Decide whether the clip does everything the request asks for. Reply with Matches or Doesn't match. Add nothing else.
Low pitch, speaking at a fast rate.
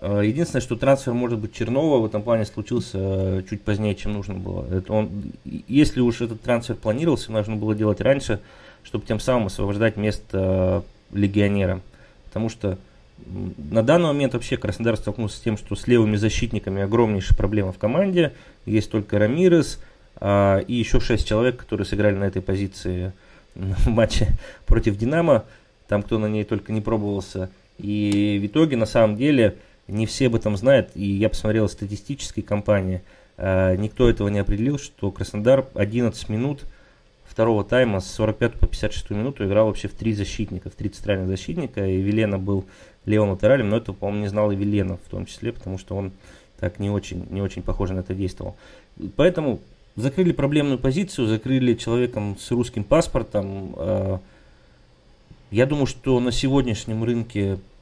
Matches